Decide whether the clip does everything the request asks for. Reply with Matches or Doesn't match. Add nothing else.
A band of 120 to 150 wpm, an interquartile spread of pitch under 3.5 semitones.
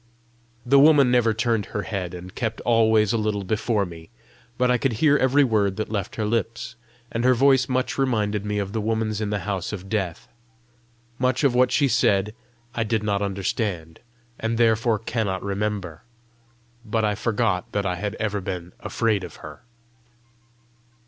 Doesn't match